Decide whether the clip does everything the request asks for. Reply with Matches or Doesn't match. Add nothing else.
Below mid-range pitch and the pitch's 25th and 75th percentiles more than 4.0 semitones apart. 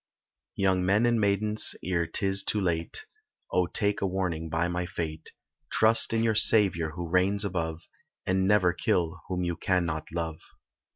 Doesn't match